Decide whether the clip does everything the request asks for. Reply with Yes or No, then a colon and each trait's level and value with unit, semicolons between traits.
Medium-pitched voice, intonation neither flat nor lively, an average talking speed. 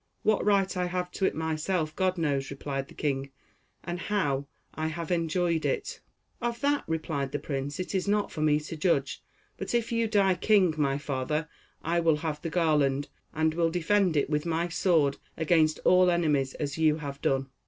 Yes: medium, 160 Hz; average, 3.6 semitones; average, 190 wpm